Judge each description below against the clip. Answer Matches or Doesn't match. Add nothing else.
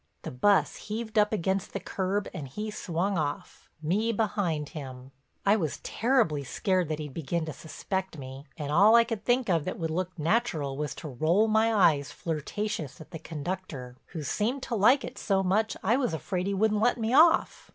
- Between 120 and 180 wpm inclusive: Doesn't match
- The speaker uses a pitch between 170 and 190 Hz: Matches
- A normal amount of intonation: Doesn't match